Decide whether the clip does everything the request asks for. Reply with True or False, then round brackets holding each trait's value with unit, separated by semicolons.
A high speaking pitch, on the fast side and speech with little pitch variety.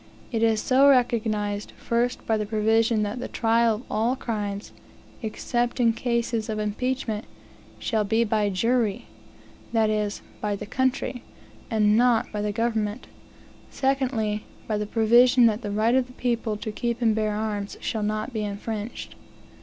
False (220 Hz; 160 wpm; 2.2 semitones)